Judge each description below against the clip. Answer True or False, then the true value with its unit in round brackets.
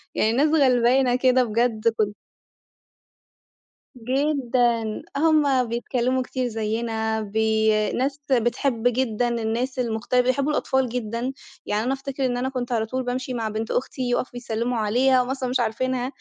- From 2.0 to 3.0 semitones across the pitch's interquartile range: True (2.4 semitones)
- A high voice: True (245 Hz)